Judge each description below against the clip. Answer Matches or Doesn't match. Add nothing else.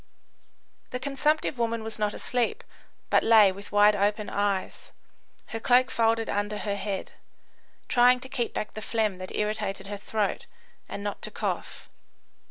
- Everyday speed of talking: Matches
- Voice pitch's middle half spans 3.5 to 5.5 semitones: Doesn't match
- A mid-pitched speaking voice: Doesn't match